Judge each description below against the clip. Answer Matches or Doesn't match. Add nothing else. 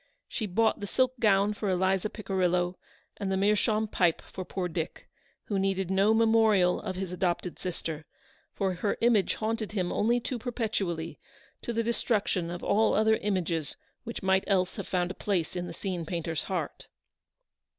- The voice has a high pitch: Matches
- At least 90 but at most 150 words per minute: Doesn't match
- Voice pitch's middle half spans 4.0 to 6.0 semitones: Doesn't match